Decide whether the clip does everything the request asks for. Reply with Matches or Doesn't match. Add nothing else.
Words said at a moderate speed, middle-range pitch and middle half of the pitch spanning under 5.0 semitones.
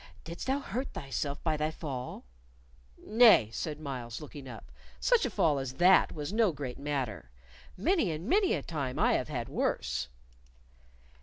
Doesn't match